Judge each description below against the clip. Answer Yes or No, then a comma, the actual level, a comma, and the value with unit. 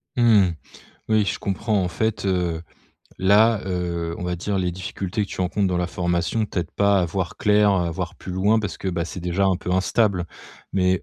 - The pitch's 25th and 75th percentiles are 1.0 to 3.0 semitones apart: Yes, narrow, 2.4 semitones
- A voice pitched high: No, very low, 95 Hz